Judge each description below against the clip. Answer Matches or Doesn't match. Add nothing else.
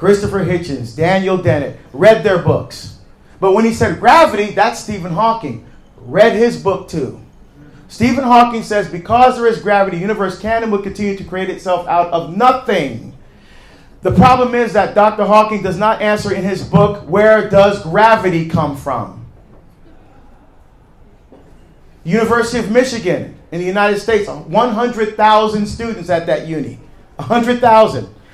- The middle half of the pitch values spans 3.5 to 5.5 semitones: Matches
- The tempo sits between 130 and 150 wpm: Matches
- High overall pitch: Matches